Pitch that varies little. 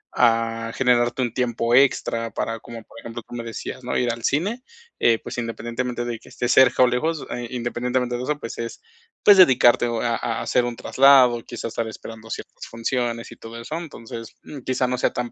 Yes: narrow, 1.6 semitones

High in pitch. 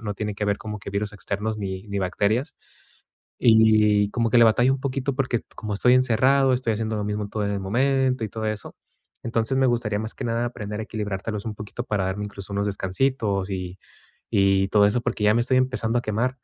No: low, 110 Hz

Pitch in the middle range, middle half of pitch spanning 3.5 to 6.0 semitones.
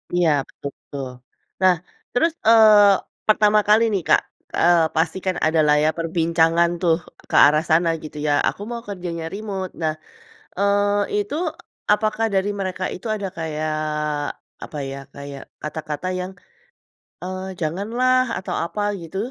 Yes: medium, 180 Hz; average, 4.0 semitones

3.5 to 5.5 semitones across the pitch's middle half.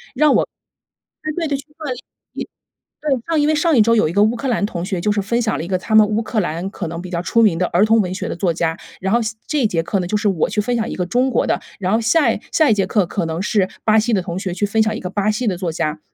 Yes: average, 4.4 semitones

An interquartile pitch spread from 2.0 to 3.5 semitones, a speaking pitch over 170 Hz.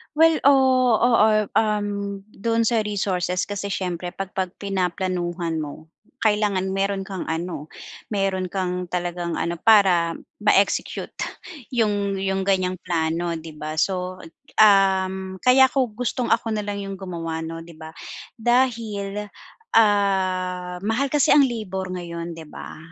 Yes: average, 3.0 semitones; high, 190 Hz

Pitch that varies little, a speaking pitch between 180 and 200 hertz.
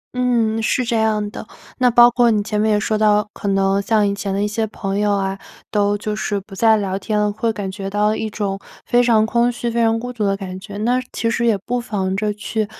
No: narrow, 2.1 semitones; high, 210 Hz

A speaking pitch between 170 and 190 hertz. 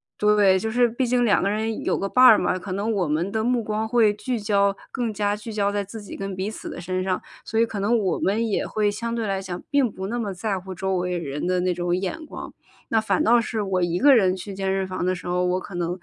No: high, 200 Hz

